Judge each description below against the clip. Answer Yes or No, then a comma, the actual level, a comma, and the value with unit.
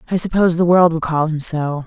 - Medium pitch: Yes, medium, 165 Hz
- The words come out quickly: Yes, fast, 255 wpm